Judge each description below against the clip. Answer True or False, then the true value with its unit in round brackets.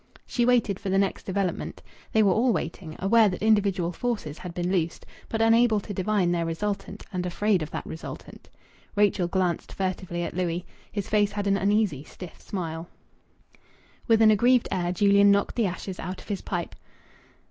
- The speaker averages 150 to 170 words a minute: False (180 wpm)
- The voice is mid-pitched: False (195 Hz)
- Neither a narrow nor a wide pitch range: True (3.1 semitones)